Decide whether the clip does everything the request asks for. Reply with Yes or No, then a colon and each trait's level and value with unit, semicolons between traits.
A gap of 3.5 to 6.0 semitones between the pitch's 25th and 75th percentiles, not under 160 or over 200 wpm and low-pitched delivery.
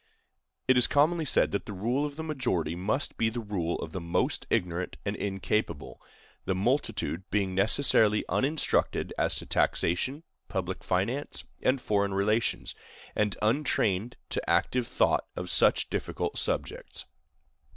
No: wide, 5.5 semitones; average, 140 wpm; low, 105 Hz